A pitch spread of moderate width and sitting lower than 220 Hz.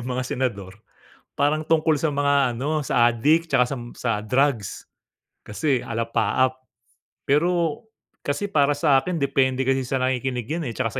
Yes: average, 3.2 semitones; low, 135 Hz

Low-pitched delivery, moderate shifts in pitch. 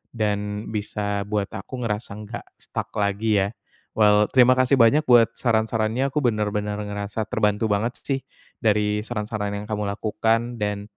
No: low, 105 Hz; narrow, 1.9 semitones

